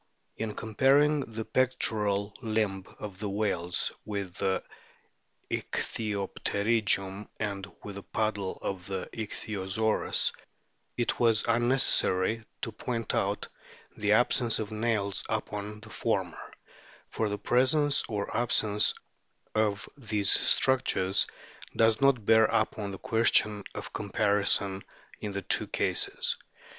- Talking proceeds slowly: Yes, slow, 115 wpm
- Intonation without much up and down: Yes, narrow, 2.2 semitones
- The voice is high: No, low, 105 Hz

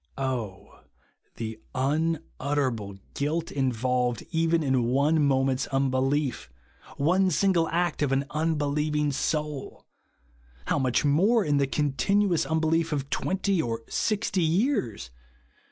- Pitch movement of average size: Yes, average, 3.7 semitones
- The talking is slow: Yes, slow, 120 wpm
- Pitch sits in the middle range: Yes, medium, 145 Hz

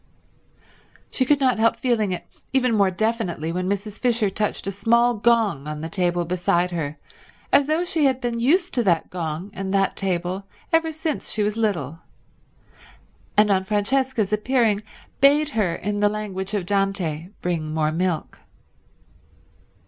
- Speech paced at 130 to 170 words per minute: Yes, average, 155 wpm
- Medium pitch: No, high, 205 Hz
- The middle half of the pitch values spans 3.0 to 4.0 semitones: No, average, 4.9 semitones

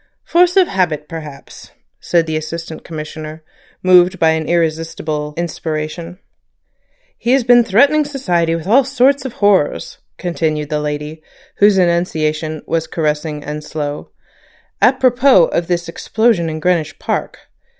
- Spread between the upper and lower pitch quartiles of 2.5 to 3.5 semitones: No, average, 4.7 semitones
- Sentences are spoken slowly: Yes, slow, 130 wpm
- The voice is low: No, medium, 165 Hz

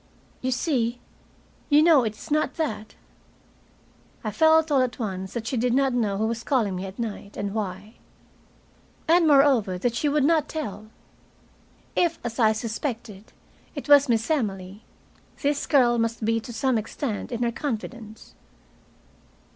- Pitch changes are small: No, average, 4.7 semitones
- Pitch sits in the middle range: No, high, 235 Hz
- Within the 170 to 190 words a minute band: No, average, 155 wpm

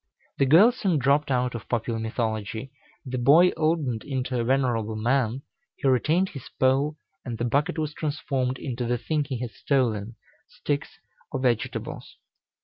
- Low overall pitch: Yes, low, 130 Hz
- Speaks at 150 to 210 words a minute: Yes, average, 155 wpm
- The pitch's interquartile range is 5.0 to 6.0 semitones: No, average, 3.6 semitones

